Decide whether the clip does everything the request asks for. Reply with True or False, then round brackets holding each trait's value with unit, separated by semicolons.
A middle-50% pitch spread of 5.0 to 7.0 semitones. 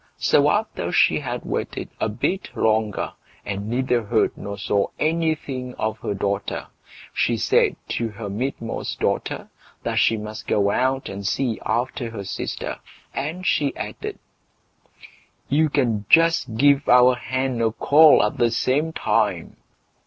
False (4.3 semitones)